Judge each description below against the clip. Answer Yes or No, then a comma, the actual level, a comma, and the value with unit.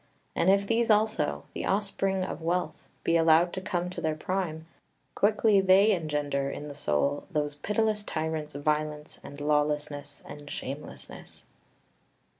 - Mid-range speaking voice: Yes, medium, 160 Hz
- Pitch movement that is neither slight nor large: Yes, average, 4.7 semitones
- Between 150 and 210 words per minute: No, average, 140 wpm